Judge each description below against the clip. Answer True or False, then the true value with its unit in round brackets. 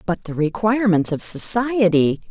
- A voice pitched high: True (195 Hz)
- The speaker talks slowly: True (130 wpm)